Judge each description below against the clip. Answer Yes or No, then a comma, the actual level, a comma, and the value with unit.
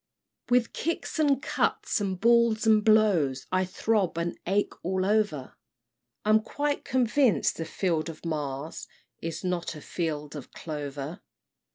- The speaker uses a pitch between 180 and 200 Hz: Yes, medium, 185 Hz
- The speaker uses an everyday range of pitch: No, wide, 5.8 semitones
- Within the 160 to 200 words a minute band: No, average, 140 wpm